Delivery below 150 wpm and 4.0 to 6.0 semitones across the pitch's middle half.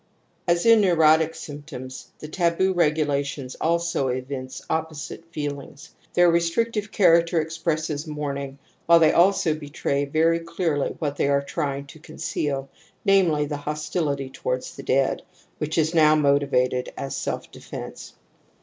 No: average, 140 wpm; average, 3.1 semitones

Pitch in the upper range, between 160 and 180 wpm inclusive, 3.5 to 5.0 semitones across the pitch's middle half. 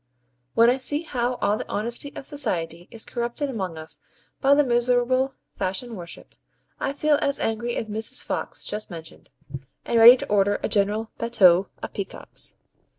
Yes: high, 230 Hz; average, 165 wpm; average, 4.1 semitones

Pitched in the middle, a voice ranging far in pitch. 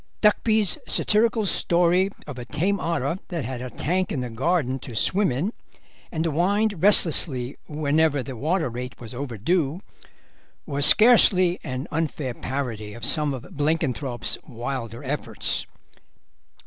Yes: medium, 150 Hz; wide, 5.9 semitones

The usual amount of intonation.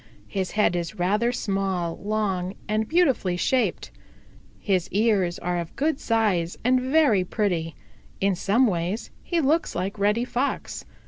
Yes: average, 4.9 semitones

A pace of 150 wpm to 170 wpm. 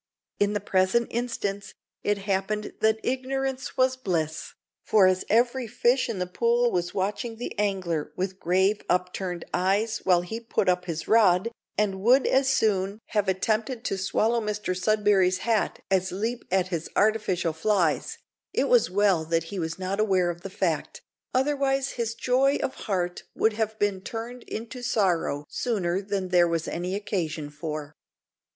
Yes: average, 160 wpm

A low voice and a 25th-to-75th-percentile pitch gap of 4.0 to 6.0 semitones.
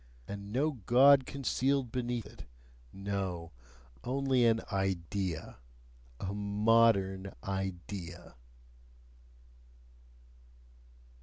Yes: low, 100 Hz; average, 4.3 semitones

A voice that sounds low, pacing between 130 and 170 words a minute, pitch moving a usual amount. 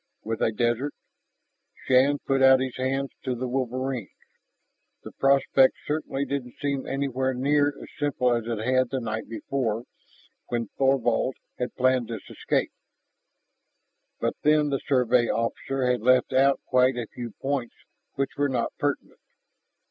No: low, 130 Hz; average, 145 wpm; narrow, 2.3 semitones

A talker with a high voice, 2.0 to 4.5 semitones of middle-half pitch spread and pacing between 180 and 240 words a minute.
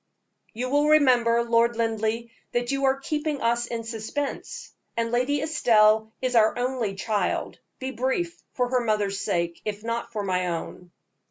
No: high, 235 Hz; average, 3.1 semitones; average, 160 wpm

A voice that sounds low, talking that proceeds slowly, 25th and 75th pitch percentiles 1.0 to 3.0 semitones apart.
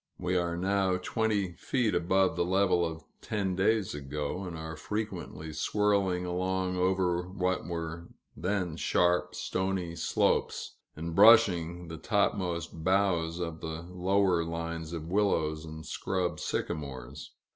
Yes: very low, 90 Hz; slow, 130 wpm; narrow, 2.5 semitones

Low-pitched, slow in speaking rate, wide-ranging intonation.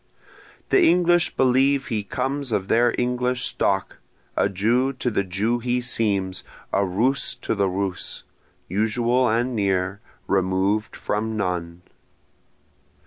No: low, 110 Hz; slow, 125 wpm; average, 4.2 semitones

